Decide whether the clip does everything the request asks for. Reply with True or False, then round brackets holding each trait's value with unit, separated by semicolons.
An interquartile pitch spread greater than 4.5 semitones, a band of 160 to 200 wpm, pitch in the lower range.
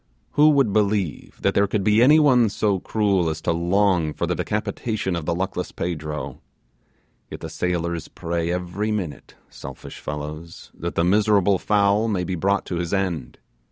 False (3.6 semitones; 170 wpm; 95 Hz)